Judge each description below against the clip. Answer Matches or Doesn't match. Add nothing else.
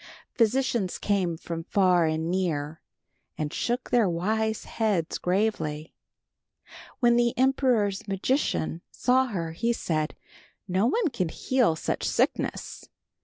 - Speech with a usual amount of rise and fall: Doesn't match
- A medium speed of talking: Doesn't match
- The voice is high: Matches